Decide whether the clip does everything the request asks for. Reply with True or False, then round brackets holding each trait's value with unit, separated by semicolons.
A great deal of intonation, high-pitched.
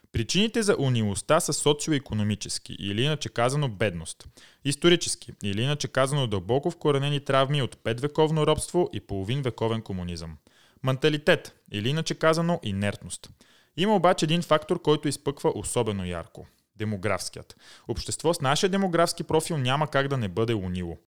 False (6.4 semitones; 135 Hz)